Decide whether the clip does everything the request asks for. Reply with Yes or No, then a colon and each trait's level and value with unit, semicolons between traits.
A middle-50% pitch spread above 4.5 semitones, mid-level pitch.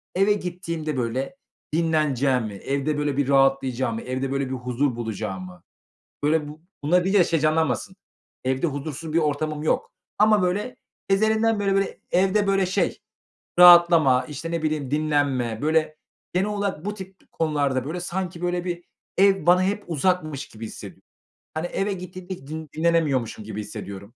Yes: average, 5.0 semitones; medium, 155 Hz